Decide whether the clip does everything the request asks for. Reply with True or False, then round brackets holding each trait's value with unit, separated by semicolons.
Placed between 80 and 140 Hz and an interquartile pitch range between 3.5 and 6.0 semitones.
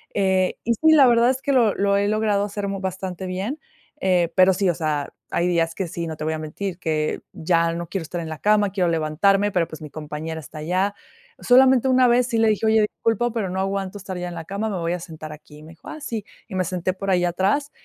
False (190 Hz; 3.9 semitones)